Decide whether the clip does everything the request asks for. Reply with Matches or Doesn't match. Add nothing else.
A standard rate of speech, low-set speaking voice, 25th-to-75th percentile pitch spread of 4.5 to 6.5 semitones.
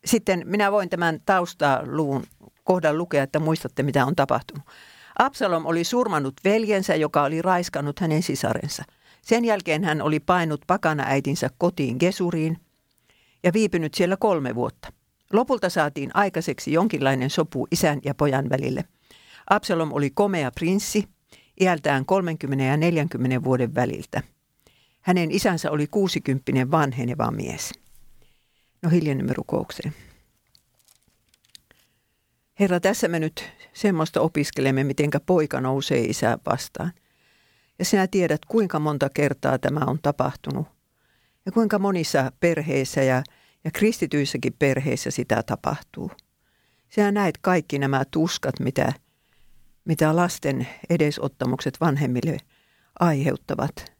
Doesn't match